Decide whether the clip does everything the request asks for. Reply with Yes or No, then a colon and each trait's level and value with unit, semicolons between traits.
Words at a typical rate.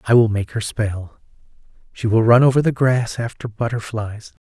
Yes: average, 175 wpm